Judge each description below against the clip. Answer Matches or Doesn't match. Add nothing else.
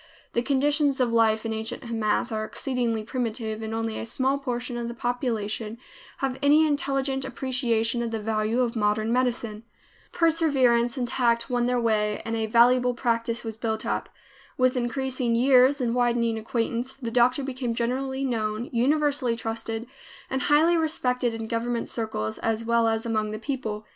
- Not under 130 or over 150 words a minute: Doesn't match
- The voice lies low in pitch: Doesn't match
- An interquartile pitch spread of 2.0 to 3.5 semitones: Matches